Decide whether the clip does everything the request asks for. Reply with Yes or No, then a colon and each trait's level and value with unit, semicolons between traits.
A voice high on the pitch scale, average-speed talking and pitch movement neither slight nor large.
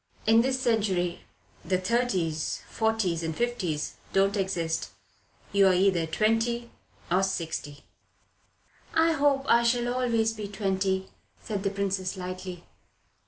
No: high, 195 Hz; slow, 115 wpm; average, 4.2 semitones